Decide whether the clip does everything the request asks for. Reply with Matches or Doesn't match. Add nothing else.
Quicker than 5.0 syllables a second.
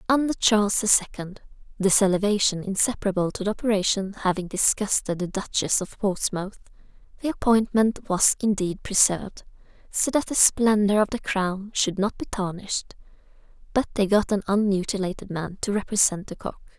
Matches